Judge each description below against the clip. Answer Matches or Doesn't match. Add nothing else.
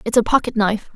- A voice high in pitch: Matches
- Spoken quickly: Matches